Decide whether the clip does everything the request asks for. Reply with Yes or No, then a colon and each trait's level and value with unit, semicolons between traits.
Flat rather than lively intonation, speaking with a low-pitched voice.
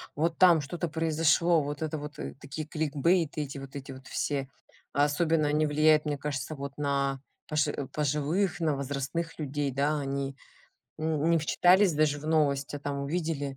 No: narrow, 2.2 semitones; medium, 150 Hz